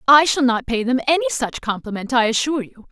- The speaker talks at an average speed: No, fast, 225 wpm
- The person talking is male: No, female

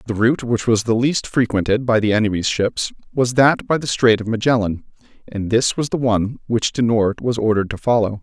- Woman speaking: No, male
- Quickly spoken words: Yes, fast, 220 wpm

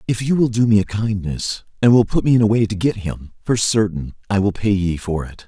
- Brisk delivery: Yes, fast, 275 wpm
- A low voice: Yes, low, 105 Hz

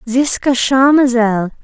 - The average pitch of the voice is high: Yes, very high, 250 Hz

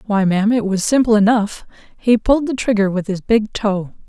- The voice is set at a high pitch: Yes, high, 215 Hz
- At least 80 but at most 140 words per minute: No, fast, 205 wpm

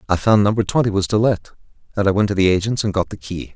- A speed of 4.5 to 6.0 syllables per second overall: No, 6.8 syllables/s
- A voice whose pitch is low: Yes, low, 100 Hz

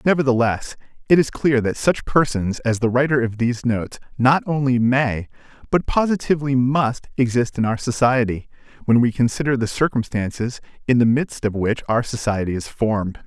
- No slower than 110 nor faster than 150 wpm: No, average, 165 wpm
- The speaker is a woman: No, male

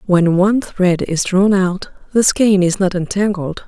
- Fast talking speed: No, average, 180 wpm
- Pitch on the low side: No, high, 190 Hz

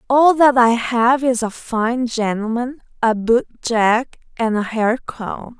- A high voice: Yes, high, 235 Hz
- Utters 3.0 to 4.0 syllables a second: Yes, 3.5 syllables/s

